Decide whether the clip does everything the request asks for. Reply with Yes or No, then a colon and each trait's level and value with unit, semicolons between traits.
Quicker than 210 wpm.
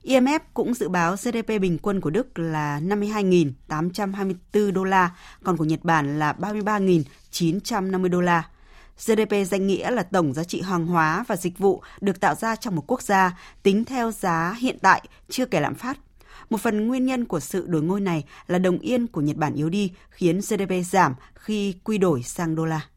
No: average, 195 wpm